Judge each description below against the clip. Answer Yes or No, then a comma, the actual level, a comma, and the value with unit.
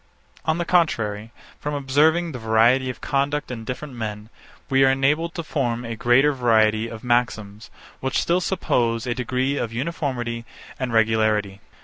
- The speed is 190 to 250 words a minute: No, average, 155 wpm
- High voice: No, low, 125 Hz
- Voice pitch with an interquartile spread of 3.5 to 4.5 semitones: Yes, average, 4.1 semitones